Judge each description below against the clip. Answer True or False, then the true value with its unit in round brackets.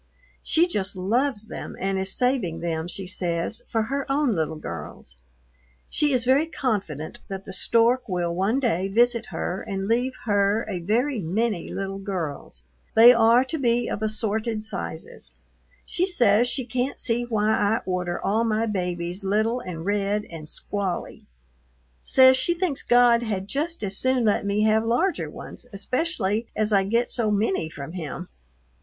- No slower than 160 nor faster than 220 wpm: True (165 wpm)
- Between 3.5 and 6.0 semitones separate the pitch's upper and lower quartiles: True (4.4 semitones)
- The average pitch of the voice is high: True (215 Hz)